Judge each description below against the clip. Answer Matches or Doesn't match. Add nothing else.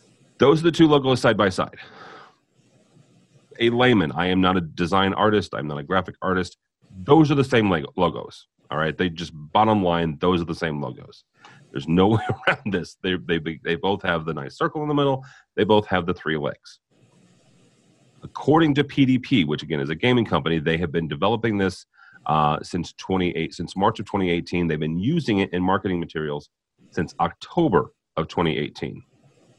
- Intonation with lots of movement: Matches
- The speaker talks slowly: Doesn't match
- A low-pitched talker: Matches